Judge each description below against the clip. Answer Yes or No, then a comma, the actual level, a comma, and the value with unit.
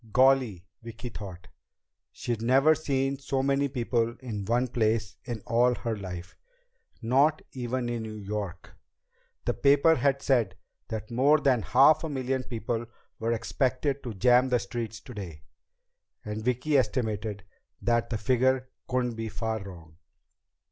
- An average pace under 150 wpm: Yes, average, 140 wpm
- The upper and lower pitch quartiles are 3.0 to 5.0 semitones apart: Yes, average, 3.3 semitones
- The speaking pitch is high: No, low, 120 Hz